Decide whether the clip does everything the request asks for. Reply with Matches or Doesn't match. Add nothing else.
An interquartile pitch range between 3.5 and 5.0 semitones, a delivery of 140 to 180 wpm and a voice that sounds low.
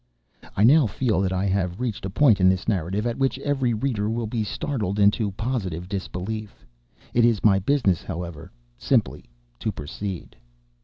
Matches